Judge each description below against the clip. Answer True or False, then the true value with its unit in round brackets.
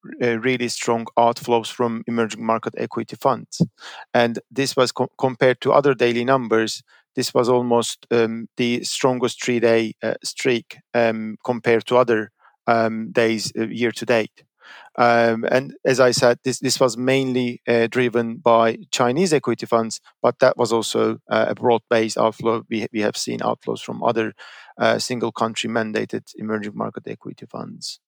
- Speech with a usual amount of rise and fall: False (1.7 semitones)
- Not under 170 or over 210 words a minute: False (160 wpm)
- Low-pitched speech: True (120 Hz)